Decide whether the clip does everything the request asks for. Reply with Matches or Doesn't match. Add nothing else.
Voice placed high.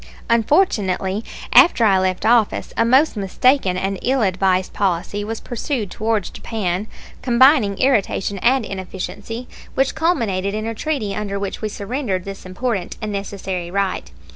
Matches